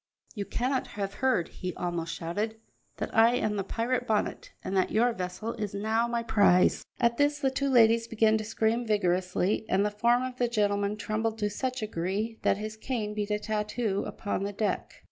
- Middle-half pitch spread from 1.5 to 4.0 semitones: Yes, narrow, 2.6 semitones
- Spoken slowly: No, average, 200 wpm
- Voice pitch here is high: Yes, high, 215 Hz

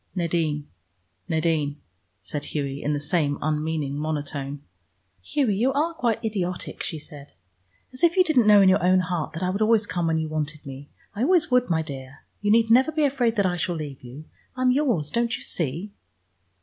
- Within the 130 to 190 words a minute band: No, average, 200 wpm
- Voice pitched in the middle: Yes, medium, 175 Hz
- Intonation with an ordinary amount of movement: No, wide, 7.3 semitones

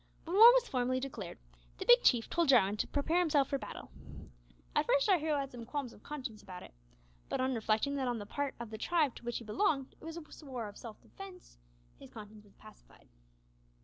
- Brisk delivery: Yes, fast, 220 wpm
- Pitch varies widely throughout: Yes, wide, 5.7 semitones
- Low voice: No, very high, 265 Hz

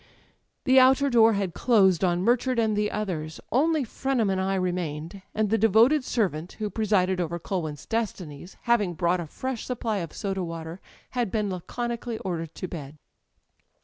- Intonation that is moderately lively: Yes, average, 4.9 semitones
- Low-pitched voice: No, high, 200 Hz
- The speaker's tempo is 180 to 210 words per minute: No, average, 170 wpm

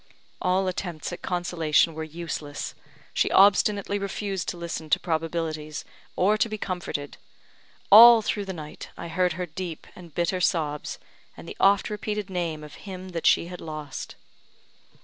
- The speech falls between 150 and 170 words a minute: Yes, average, 155 wpm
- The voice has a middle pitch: Yes, medium, 175 Hz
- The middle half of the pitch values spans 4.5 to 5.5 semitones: No, average, 3.4 semitones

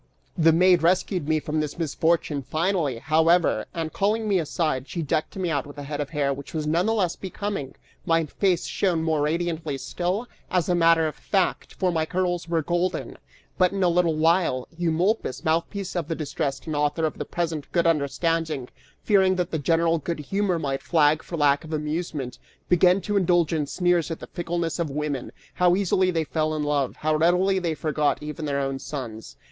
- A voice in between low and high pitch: Yes, medium, 165 Hz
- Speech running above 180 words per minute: Yes, average, 195 wpm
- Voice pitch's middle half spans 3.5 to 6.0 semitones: No, average, 2.9 semitones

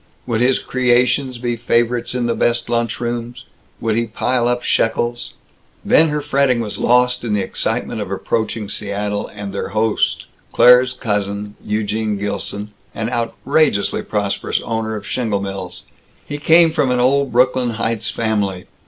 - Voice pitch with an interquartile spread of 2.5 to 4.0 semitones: Yes, average, 3.0 semitones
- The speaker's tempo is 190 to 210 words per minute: No, average, 155 wpm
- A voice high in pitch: No, low, 115 Hz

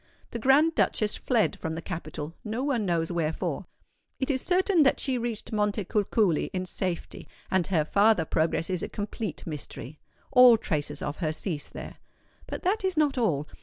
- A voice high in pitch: Yes, high, 205 Hz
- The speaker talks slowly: No, average, 165 wpm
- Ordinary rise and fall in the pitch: No, wide, 7.4 semitones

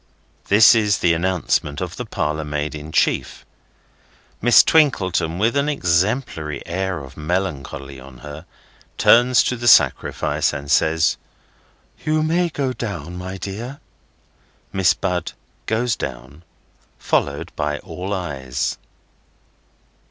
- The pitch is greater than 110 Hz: No, very low, 90 Hz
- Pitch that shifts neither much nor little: No, wide, 7.0 semitones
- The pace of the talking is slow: Yes, slow, 120 wpm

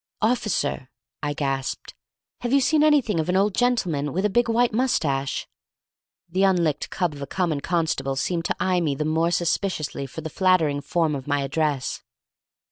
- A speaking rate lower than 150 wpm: No, average, 175 wpm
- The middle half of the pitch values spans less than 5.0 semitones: No, wide, 5.4 semitones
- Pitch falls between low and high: Yes, medium, 165 Hz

